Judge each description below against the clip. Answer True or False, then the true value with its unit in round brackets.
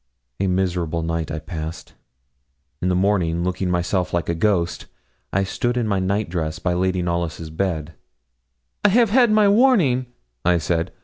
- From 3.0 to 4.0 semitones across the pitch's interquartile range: True (3.6 semitones)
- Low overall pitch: True (90 Hz)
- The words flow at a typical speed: True (165 wpm)